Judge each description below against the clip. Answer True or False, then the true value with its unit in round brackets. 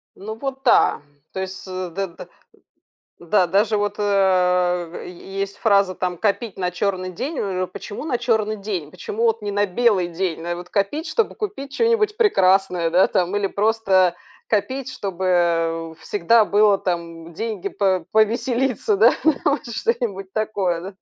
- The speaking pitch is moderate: False (195 Hz)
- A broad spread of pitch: False (3.6 semitones)